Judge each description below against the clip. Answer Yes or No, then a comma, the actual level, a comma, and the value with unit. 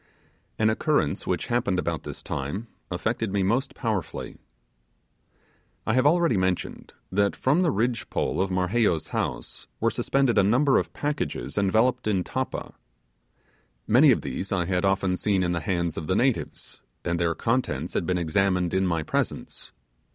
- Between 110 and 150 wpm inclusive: No, average, 160 wpm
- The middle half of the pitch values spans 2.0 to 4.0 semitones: No, average, 4.8 semitones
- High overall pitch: No, low, 100 Hz